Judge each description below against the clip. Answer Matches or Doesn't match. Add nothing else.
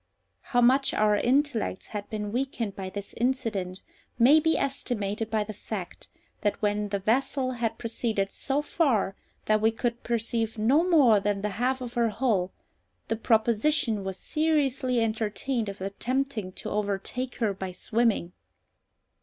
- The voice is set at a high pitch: Matches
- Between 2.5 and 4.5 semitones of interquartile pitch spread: Matches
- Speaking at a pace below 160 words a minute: Matches